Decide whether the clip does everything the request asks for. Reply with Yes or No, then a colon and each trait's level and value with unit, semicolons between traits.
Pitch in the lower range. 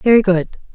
No: high, 195 Hz